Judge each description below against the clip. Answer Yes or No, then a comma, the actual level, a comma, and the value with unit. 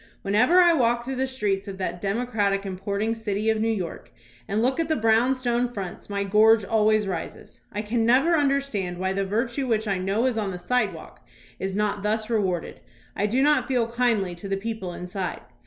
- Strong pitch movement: No, average, 3.6 semitones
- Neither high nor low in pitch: No, high, 215 Hz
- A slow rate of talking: No, average, 200 wpm